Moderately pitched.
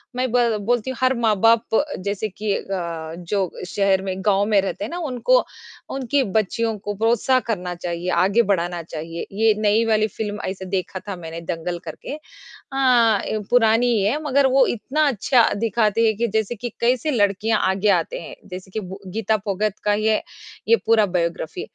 No: high, 215 Hz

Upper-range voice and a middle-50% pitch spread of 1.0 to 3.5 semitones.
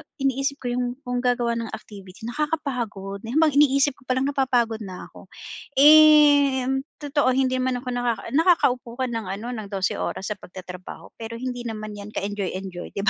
No: high, 245 Hz; average, 4.2 semitones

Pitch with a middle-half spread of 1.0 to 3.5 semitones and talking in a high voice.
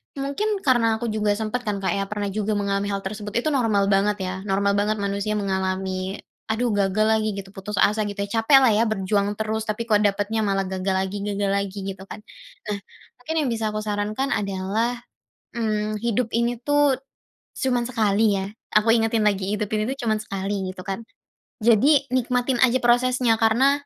Yes: average, 2.8 semitones; high, 215 Hz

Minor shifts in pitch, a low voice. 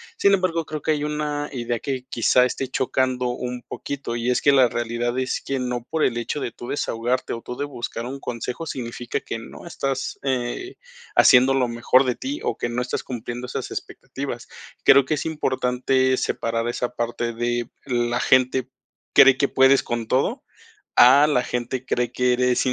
Yes: narrow, 2.2 semitones; low, 125 Hz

